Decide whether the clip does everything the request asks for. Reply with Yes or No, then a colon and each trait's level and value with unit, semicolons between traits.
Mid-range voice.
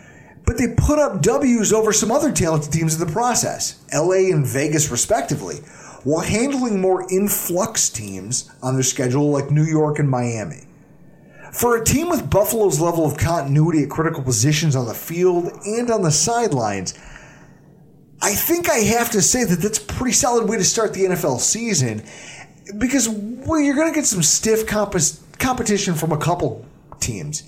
Yes: medium, 175 Hz